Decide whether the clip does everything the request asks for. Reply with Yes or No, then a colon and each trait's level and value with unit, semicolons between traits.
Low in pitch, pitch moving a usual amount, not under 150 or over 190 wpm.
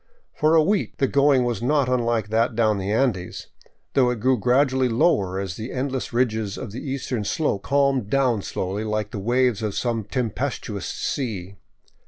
Yes: low, 120 Hz; average, 3.8 semitones; average, 175 wpm